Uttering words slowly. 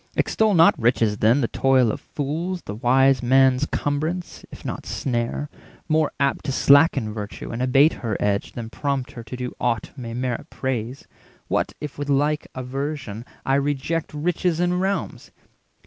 No: average, 165 wpm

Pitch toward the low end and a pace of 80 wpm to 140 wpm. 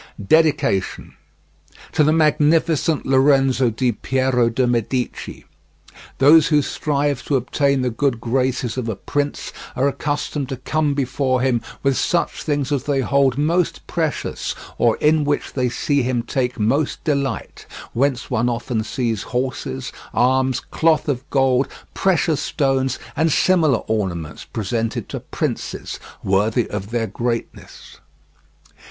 Yes: low, 130 Hz; slow, 135 wpm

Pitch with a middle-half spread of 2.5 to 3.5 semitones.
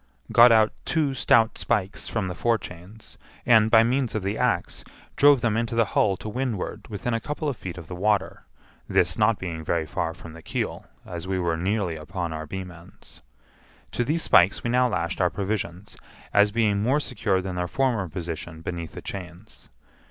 No: average, 4.7 semitones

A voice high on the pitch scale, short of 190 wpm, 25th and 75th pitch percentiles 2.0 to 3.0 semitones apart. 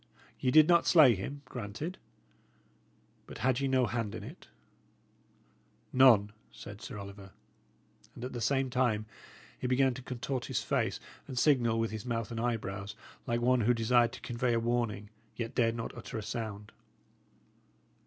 No: low, 120 Hz; average, 165 wpm; narrow, 2.6 semitones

